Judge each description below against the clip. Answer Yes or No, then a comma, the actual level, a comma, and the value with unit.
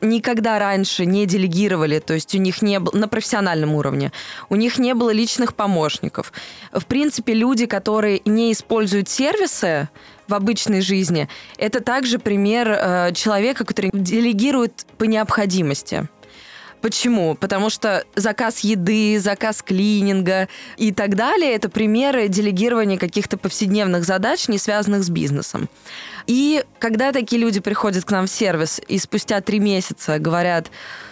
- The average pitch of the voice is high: Yes, high, 210 Hz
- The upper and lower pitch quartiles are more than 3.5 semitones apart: No, average, 3.0 semitones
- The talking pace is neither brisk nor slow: Yes, average, 140 wpm